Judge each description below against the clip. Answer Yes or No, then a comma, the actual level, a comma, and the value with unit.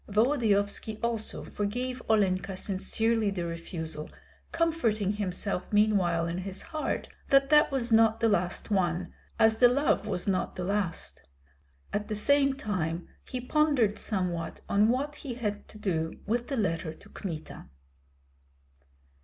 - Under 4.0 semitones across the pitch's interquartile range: No, average, 4.6 semitones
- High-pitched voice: Yes, high, 210 Hz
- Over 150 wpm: No, average, 140 wpm